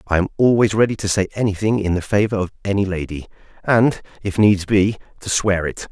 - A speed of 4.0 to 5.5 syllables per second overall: No, 5.8 syllables/s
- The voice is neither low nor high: No, low, 100 Hz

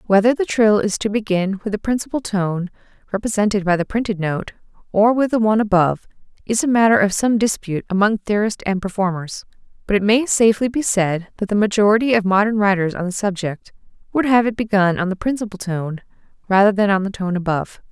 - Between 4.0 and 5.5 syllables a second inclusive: No, 5.7 syllables/s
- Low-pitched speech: No, high, 205 Hz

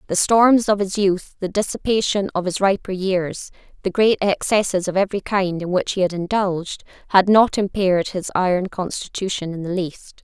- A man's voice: No, female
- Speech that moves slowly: No, average, 180 wpm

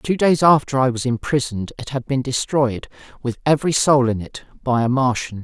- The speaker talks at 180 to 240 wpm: Yes, average, 200 wpm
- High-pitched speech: No, low, 130 Hz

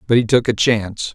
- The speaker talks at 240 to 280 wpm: Yes, fast, 260 wpm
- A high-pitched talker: No, low, 110 Hz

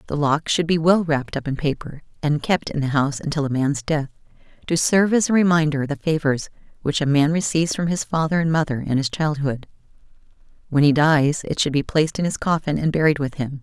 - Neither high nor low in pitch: Yes, medium, 150 Hz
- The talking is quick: Yes, fast, 230 wpm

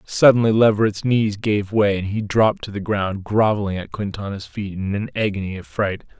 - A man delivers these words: Yes, male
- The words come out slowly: No, average, 195 wpm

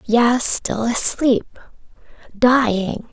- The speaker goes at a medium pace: No, slow, 60 wpm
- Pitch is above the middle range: Yes, high, 235 Hz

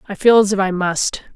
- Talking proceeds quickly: Yes, fast, 265 wpm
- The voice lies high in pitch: Yes, high, 195 Hz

